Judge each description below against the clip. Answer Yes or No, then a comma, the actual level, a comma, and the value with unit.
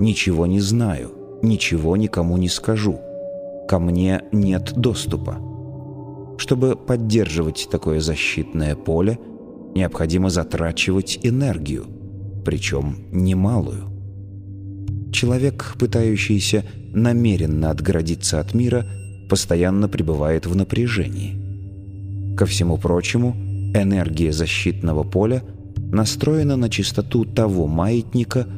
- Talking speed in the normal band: No, slow, 90 wpm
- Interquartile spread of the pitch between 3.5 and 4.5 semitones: Yes, average, 3.9 semitones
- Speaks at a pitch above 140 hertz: No, low, 100 Hz